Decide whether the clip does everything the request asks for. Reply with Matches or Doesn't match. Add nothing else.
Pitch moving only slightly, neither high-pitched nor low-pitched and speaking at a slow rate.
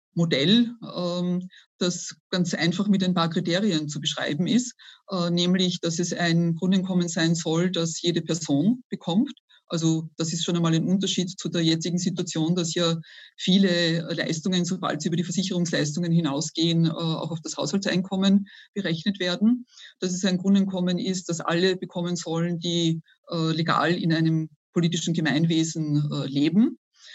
Doesn't match